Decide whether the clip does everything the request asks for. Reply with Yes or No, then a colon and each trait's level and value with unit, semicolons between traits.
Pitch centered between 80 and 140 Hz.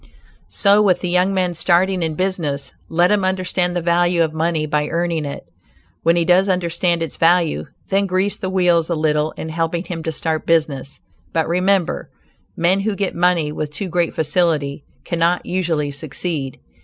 No: medium, 170 Hz